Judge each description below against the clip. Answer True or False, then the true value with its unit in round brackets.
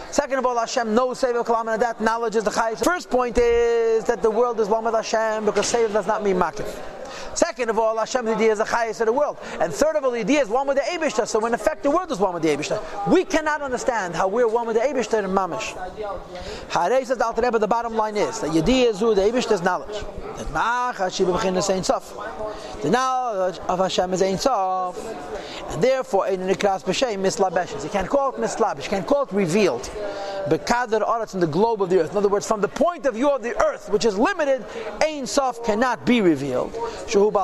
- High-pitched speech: True (225 Hz)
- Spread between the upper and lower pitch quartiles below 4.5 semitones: True (3.9 semitones)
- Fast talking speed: True (210 wpm)